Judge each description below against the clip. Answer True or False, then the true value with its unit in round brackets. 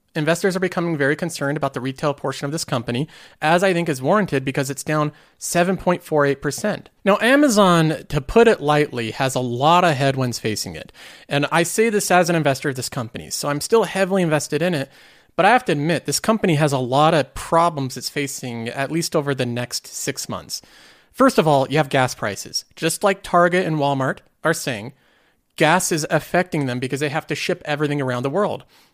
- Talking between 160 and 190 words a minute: False (205 wpm)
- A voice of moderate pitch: True (150 Hz)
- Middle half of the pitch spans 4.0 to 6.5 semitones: True (4.3 semitones)